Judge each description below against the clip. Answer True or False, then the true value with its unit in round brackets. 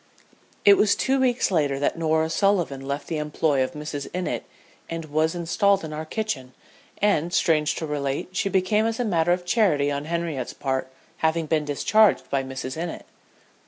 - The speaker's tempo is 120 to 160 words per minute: False (175 wpm)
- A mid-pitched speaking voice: True (160 Hz)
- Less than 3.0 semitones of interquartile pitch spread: False (4.3 semitones)